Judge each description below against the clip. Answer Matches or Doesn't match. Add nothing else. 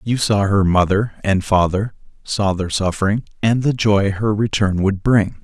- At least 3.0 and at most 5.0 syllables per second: Matches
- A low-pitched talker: Matches